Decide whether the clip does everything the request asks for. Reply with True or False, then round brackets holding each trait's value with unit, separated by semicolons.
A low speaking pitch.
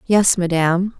False (185 Hz)